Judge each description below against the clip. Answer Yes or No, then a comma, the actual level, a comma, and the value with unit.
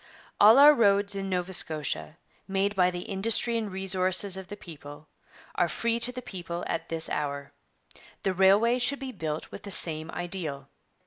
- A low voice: No, high, 190 Hz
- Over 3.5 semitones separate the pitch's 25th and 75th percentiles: Yes, average, 3.9 semitones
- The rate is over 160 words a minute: Yes, average, 175 wpm